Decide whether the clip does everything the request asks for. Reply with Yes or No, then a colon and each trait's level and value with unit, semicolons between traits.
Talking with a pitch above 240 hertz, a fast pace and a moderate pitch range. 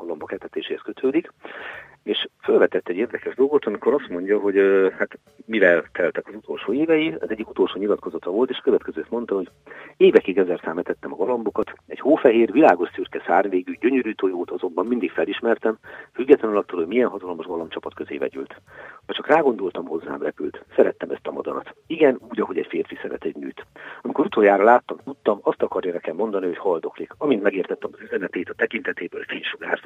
Yes: very high, 400 Hz; fast, 165 wpm; average, 3.0 semitones